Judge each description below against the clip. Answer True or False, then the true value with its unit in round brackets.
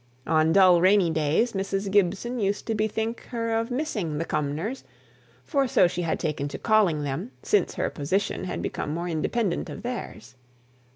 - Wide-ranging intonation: True (5.9 semitones)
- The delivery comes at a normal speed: True (170 wpm)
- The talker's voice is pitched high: True (195 Hz)